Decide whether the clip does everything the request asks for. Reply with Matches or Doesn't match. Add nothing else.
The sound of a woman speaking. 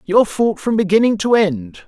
Doesn't match